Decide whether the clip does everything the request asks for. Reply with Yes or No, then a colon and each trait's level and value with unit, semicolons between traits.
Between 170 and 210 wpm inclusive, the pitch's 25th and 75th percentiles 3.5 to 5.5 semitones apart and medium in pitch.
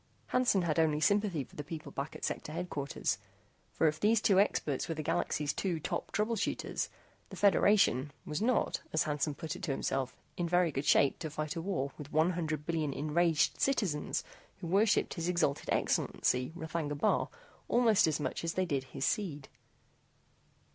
Yes: average, 180 wpm; average, 3.8 semitones; medium, 160 Hz